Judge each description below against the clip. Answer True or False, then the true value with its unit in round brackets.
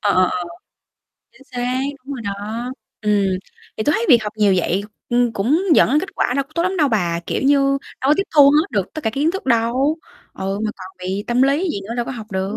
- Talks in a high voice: True (240 Hz)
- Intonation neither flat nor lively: False (5.8 semitones)